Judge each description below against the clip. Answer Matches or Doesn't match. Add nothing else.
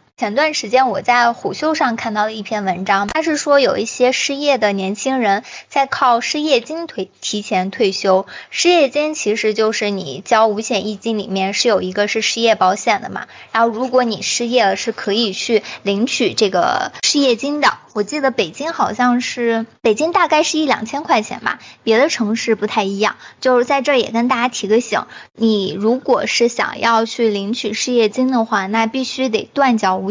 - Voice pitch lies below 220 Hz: Doesn't match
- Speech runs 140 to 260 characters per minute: Doesn't match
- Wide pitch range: Doesn't match